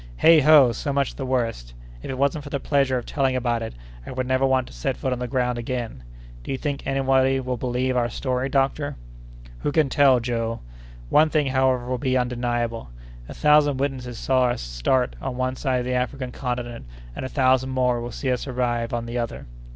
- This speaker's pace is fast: Yes, fast, 215 wpm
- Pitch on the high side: No, low, 130 Hz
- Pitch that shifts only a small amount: Yes, narrow, 1.8 semitones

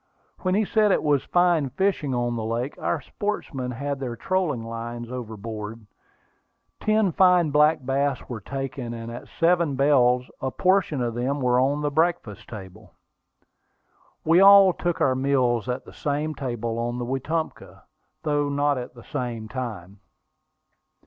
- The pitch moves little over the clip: No, average, 4.7 semitones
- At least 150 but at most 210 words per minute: Yes, average, 155 wpm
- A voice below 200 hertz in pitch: Yes, low, 135 Hz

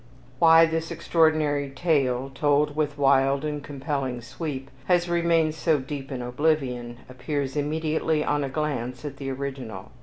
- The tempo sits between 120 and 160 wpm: Yes, average, 145 wpm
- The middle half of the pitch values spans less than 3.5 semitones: Yes, average, 2.8 semitones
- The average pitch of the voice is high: No, medium, 145 Hz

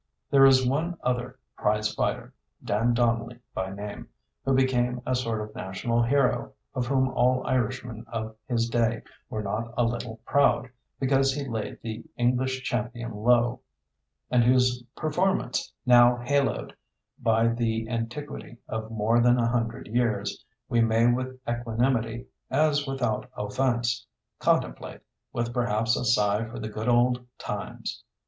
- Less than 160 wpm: Yes, average, 140 wpm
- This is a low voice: Yes, low, 120 Hz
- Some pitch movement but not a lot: No, narrow, 2.0 semitones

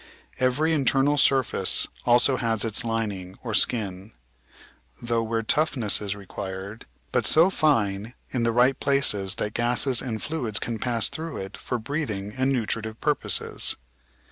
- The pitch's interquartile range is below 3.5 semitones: No, average, 4.2 semitones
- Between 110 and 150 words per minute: Yes, average, 145 wpm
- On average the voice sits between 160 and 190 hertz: No, low, 115 Hz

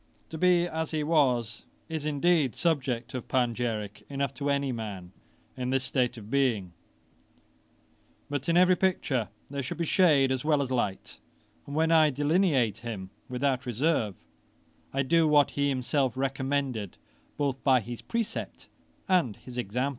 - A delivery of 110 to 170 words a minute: Yes, average, 155 wpm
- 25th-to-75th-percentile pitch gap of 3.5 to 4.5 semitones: Yes, average, 4.0 semitones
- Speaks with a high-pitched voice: No, low, 135 Hz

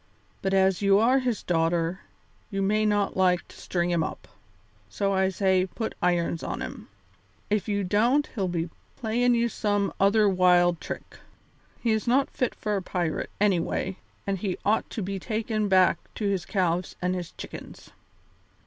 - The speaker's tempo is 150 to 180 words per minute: Yes, average, 170 wpm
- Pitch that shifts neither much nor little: Yes, average, 3.0 semitones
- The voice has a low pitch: No, high, 195 Hz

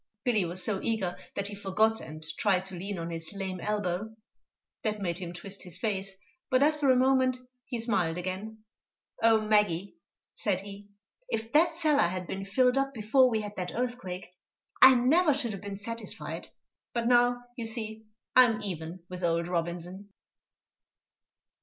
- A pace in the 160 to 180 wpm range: Yes, average, 165 wpm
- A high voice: Yes, high, 205 Hz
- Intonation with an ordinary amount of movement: Yes, average, 4.7 semitones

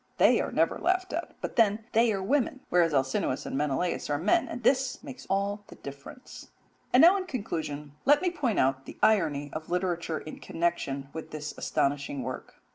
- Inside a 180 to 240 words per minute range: Yes, average, 190 wpm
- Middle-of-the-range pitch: Yes, medium, 180 Hz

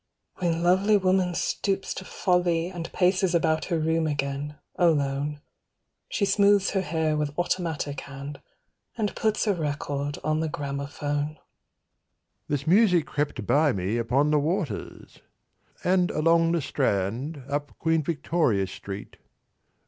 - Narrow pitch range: No, average, 3.8 semitones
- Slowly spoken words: Yes, slow, 130 wpm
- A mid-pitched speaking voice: Yes, medium, 155 Hz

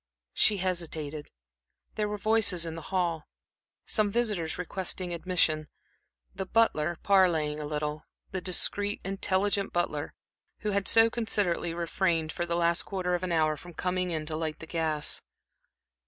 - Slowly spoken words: No, average, 150 wpm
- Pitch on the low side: No, medium, 175 Hz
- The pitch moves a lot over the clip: No, average, 3.5 semitones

